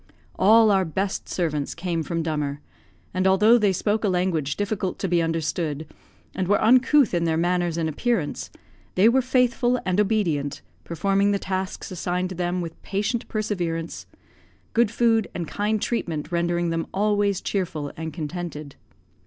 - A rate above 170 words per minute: No, average, 155 wpm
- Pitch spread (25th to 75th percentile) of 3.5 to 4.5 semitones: Yes, average, 4.0 semitones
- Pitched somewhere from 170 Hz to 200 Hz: Yes, medium, 185 Hz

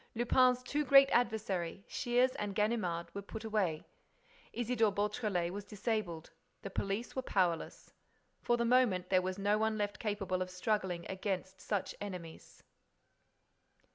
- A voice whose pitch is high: Yes, high, 205 Hz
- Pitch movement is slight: No, average, 3.9 semitones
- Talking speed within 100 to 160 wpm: Yes, average, 140 wpm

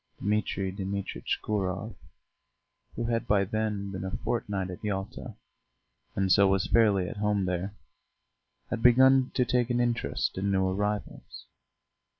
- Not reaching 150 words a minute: Yes, average, 140 wpm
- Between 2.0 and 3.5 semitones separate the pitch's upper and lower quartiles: Yes, average, 2.9 semitones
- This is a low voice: Yes, low, 100 Hz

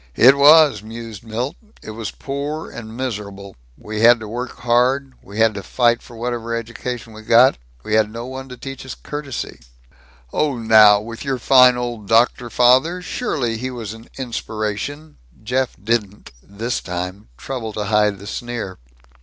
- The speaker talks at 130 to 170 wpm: Yes, average, 165 wpm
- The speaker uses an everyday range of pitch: Yes, average, 3.0 semitones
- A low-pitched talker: Yes, low, 115 Hz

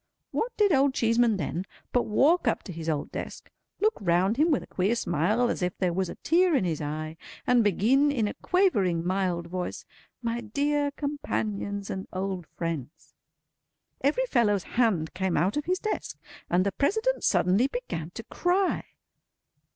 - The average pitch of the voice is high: Yes, high, 215 Hz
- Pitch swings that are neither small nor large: No, wide, 7.9 semitones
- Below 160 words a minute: No, average, 170 wpm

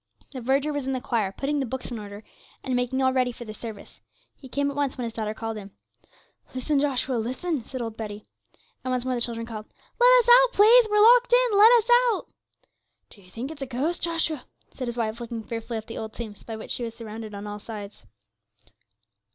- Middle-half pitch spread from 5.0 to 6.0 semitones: No, average, 4.4 semitones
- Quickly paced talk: Yes, fast, 225 wpm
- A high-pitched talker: Yes, very high, 250 Hz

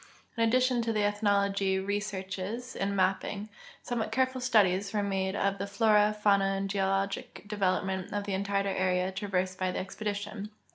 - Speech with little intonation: Yes, narrow, 1.7 semitones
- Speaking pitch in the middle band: No, high, 200 Hz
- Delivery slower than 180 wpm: Yes, average, 160 wpm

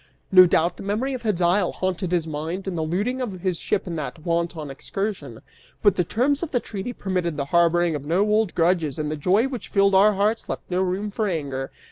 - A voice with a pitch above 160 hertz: Yes, medium, 185 Hz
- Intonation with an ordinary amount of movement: Yes, average, 3.9 semitones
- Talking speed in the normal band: No, fast, 220 wpm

